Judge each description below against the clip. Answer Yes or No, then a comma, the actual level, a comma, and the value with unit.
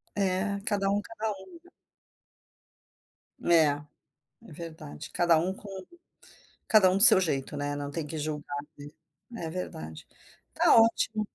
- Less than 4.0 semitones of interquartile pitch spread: No, wide, 5.5 semitones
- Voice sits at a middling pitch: Yes, medium, 175 Hz